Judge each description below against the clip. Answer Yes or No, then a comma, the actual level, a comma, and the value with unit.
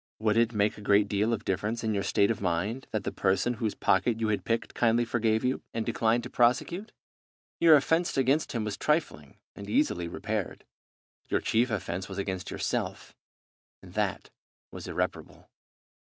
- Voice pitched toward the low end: Yes, low, 110 Hz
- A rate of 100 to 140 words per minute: No, average, 175 wpm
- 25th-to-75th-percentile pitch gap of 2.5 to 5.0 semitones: Yes, average, 3.0 semitones